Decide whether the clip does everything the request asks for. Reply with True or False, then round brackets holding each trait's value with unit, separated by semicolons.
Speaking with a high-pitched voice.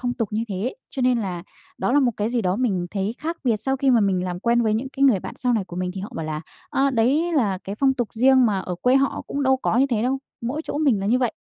True (235 Hz)